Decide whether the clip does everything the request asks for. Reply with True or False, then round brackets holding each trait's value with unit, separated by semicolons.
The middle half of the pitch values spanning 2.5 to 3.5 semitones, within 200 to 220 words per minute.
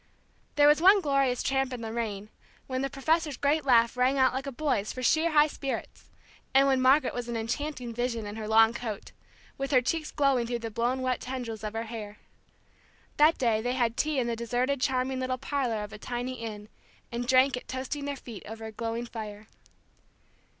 True (3.1 semitones; 205 wpm)